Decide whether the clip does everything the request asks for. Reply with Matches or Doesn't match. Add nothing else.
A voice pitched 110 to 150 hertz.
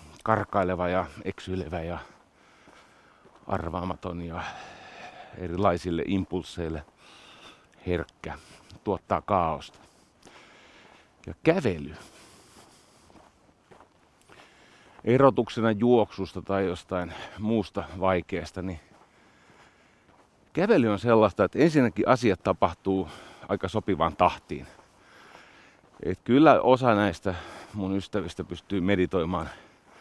Doesn't match